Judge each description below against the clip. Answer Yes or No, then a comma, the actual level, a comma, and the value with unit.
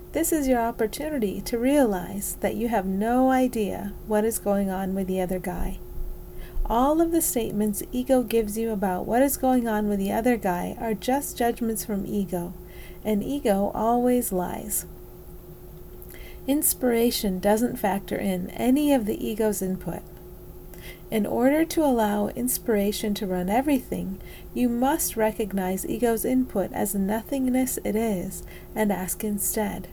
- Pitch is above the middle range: Yes, high, 220 Hz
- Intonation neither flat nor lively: Yes, average, 4.0 semitones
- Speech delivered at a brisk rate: No, average, 145 wpm